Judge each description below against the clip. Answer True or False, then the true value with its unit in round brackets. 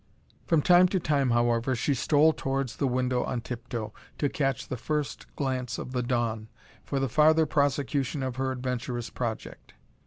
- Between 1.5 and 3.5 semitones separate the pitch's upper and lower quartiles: True (2.9 semitones)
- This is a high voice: False (130 Hz)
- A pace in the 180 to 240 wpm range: False (165 wpm)